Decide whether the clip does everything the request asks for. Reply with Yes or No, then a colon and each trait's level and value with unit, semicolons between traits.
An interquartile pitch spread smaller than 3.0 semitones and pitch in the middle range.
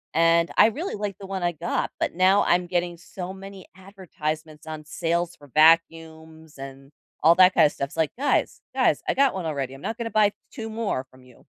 No: average, 3.8 semitones; medium, 170 Hz